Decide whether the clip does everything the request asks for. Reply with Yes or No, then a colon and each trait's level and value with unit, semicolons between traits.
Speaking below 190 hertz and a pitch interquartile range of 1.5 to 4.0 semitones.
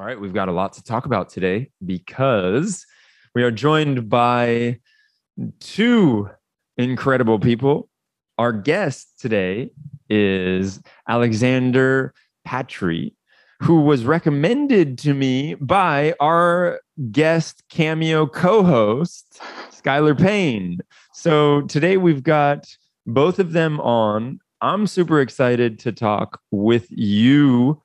No: medium, 140 Hz; average, 5.1 semitones